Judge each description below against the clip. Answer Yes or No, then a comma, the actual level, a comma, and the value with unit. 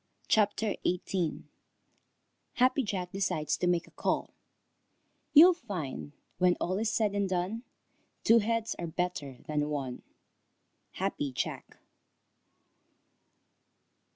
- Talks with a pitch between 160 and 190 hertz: Yes, medium, 185 Hz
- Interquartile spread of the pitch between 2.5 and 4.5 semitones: No, average, 5.3 semitones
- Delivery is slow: Yes, slow, 110 wpm